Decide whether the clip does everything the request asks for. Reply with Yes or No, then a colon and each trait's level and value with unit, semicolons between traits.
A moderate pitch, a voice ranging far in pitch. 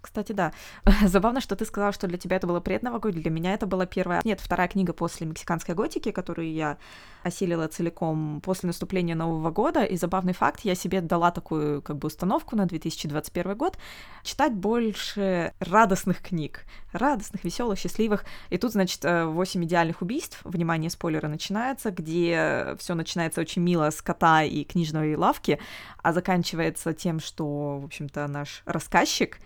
No: medium, 175 Hz; average, 3.2 semitones